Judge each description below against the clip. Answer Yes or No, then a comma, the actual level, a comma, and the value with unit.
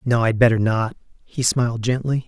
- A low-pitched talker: Yes, low, 120 Hz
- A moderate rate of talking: Yes, average, 185 wpm